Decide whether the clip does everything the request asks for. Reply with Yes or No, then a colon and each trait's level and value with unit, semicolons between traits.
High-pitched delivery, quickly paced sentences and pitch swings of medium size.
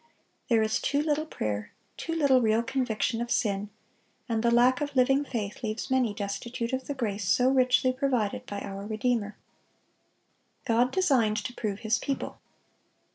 No: high, 235 Hz; average, 160 wpm; average, 3.5 semitones